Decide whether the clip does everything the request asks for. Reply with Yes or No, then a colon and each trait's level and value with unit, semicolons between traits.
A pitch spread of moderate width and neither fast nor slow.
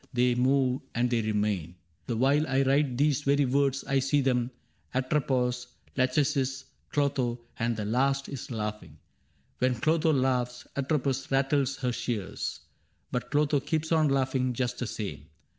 No: narrow, 2.2 semitones; average, 150 wpm